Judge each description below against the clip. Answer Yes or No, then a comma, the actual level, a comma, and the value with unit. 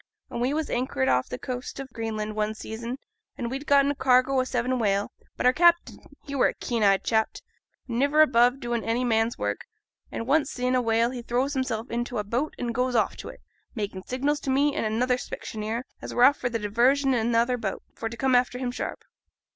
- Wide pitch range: No, narrow, 2.6 semitones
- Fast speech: Yes, fast, 220 wpm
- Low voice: No, high, 245 Hz